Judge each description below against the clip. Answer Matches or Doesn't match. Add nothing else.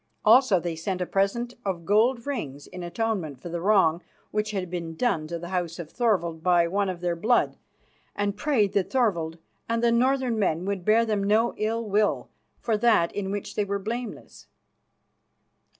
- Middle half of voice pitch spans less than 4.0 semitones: Doesn't match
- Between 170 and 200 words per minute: Matches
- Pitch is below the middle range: Doesn't match